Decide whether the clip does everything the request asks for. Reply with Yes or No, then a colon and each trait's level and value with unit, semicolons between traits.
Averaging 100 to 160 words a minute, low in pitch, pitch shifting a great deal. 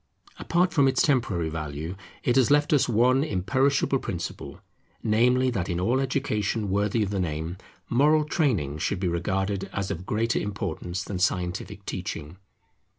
Yes: average, 150 wpm; low, 105 Hz; wide, 6.5 semitones